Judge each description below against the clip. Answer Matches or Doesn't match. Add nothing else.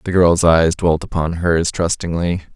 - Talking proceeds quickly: Doesn't match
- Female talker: Doesn't match